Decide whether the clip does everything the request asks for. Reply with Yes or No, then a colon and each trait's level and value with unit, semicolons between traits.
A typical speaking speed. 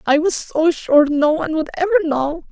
No: fast, 215 wpm